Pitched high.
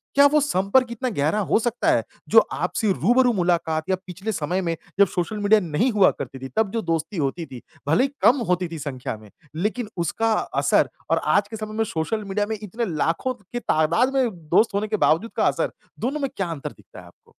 Yes: high, 200 Hz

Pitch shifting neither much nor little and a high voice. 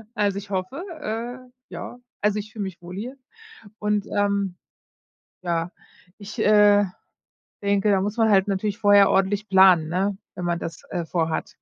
No: narrow, 2.0 semitones; high, 200 Hz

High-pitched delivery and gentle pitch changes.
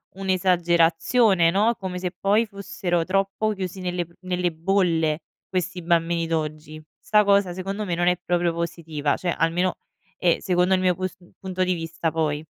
No: medium, 180 Hz; narrow, 2.3 semitones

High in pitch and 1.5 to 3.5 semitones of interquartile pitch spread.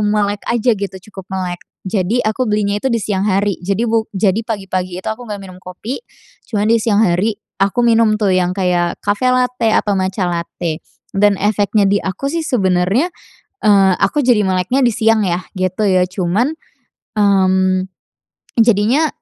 Yes: high, 205 Hz; average, 3.1 semitones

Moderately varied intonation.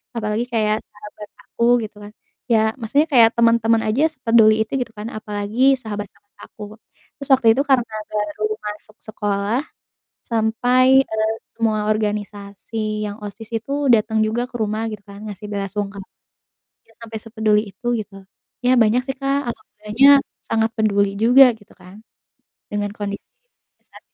No: narrow, 1.9 semitones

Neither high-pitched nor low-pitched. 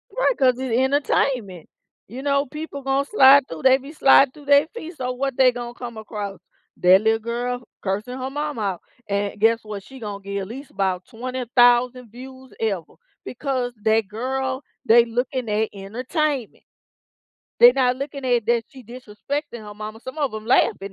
No: high, 245 Hz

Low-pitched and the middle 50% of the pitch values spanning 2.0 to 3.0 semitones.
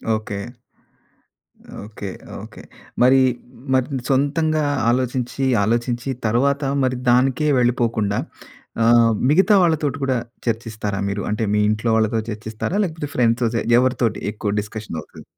No: low, 120 Hz; average, 3.4 semitones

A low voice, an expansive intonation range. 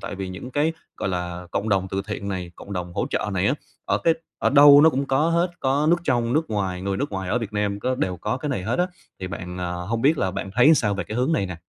Yes: low, 105 Hz; wide, 6.8 semitones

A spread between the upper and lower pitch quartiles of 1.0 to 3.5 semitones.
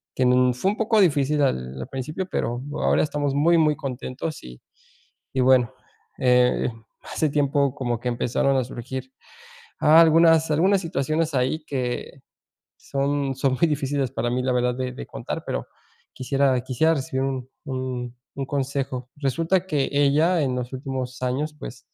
Yes: average, 3.1 semitones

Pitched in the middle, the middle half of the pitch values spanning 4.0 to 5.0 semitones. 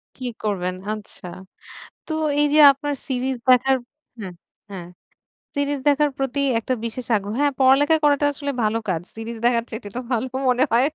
No: very high, 255 Hz; average, 4.3 semitones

